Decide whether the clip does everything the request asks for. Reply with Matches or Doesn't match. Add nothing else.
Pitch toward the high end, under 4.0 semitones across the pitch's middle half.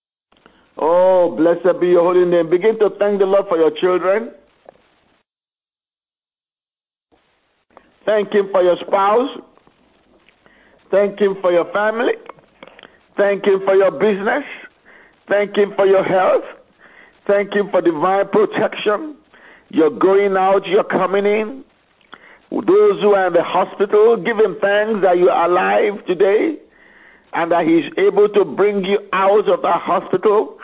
Matches